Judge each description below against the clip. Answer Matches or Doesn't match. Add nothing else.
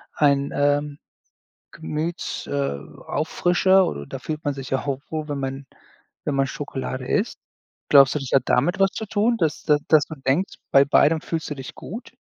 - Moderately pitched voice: Matches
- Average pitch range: Matches